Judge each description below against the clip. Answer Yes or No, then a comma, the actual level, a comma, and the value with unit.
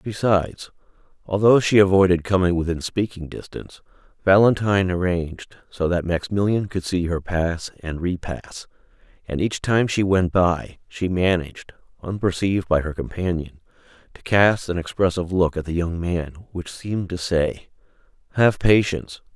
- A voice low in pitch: Yes, very low, 90 Hz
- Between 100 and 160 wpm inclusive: Yes, average, 145 wpm